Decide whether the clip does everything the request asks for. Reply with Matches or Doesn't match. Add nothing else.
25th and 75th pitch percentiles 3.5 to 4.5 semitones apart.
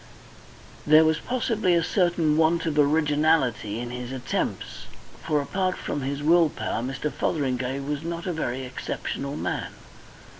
Matches